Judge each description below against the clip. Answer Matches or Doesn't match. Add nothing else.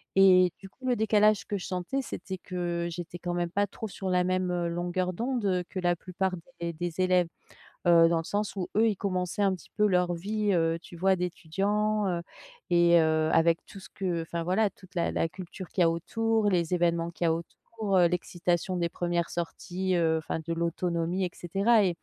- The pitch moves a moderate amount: Doesn't match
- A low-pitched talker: Doesn't match